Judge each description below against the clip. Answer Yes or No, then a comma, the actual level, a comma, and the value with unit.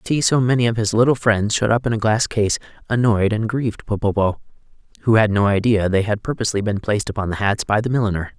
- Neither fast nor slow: No, fast, 235 wpm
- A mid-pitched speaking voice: No, low, 110 Hz